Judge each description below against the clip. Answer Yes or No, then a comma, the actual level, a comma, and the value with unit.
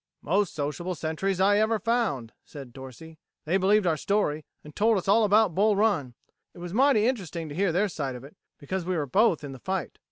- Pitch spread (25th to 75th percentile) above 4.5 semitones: Yes, wide, 5.6 semitones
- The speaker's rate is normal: No, fast, 215 wpm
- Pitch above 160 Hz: Yes, medium, 185 Hz